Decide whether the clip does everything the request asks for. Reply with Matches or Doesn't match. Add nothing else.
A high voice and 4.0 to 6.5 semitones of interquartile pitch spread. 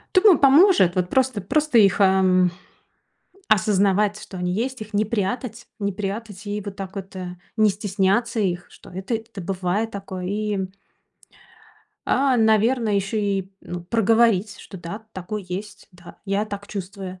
Doesn't match